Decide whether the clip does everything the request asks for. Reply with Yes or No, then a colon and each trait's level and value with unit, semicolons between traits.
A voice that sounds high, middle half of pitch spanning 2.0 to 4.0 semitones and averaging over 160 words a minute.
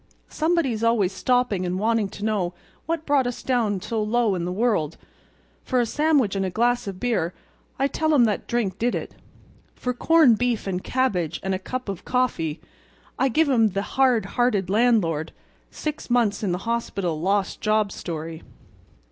No: high, 220 Hz; average, 4.6 semitones; average, 175 wpm